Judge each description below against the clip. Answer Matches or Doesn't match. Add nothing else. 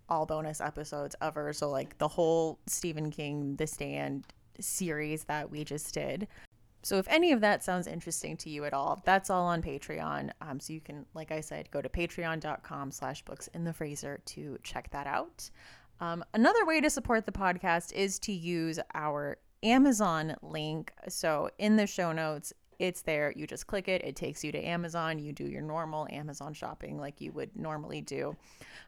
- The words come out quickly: Doesn't match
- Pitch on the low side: Doesn't match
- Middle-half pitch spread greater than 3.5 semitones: Doesn't match